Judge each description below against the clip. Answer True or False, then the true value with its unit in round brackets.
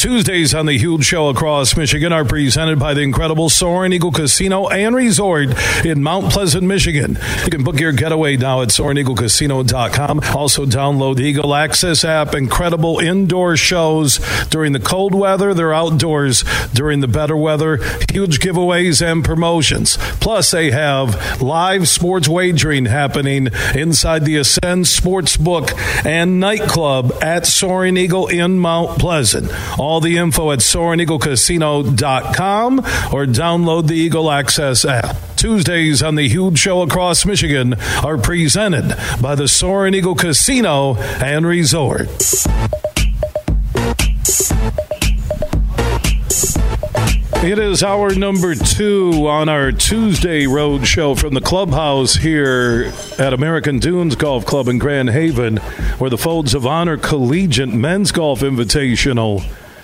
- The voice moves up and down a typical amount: True (4.4 semitones)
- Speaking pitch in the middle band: True (155 Hz)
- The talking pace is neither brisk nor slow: False (130 wpm)